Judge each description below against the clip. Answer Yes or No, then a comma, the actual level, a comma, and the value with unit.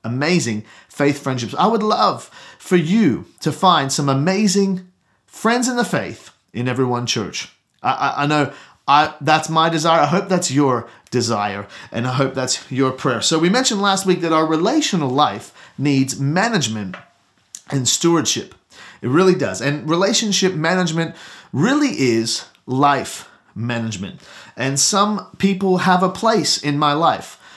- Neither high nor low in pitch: Yes, medium, 150 Hz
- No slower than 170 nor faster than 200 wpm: No, average, 155 wpm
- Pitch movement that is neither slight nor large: No, wide, 6.2 semitones